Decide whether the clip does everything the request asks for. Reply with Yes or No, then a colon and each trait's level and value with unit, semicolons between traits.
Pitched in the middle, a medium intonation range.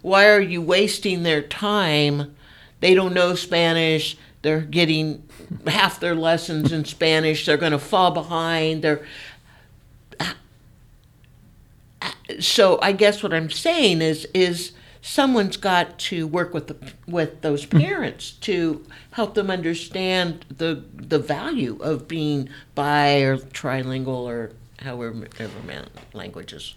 Yes: medium, 155 Hz; average, 3.6 semitones